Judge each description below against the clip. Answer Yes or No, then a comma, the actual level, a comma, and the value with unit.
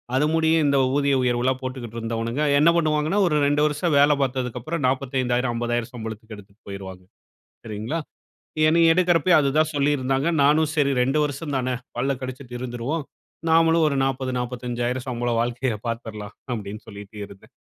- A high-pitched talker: No, low, 130 Hz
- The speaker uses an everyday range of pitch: Yes, average, 3.9 semitones